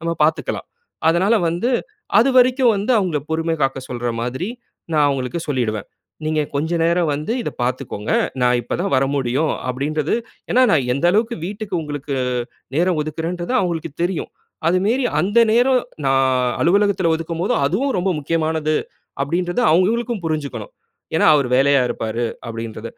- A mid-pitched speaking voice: Yes, medium, 165 Hz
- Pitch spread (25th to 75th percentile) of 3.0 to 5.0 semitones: No, wide, 5.4 semitones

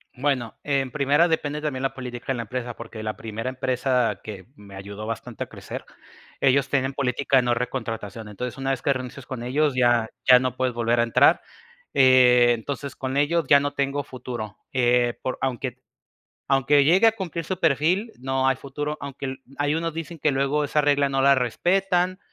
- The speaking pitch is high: No, low, 130 Hz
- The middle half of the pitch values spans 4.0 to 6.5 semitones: No, average, 2.9 semitones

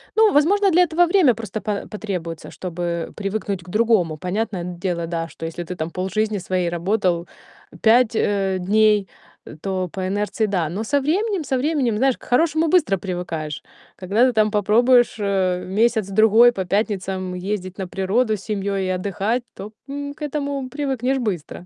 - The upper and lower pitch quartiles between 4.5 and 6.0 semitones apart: Yes, average, 5.0 semitones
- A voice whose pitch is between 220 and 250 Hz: No, high, 205 Hz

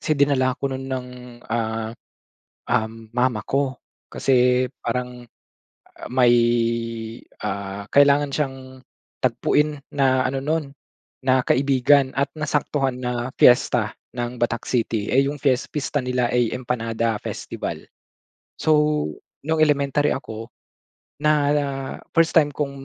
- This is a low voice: Yes, low, 130 Hz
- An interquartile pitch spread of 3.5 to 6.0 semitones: No, average, 2.8 semitones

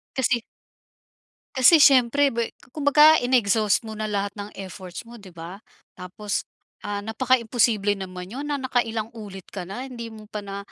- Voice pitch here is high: Yes, high, 220 Hz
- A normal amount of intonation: Yes, average, 4.0 semitones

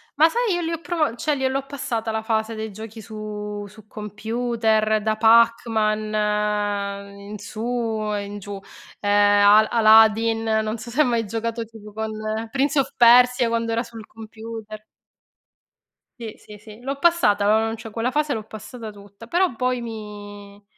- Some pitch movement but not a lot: No, narrow, 2.0 semitones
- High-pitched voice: Yes, high, 220 Hz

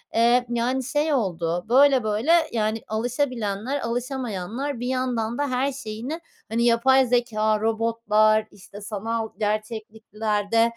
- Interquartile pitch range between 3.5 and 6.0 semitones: No, average, 2.8 semitones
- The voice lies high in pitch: Yes, high, 230 Hz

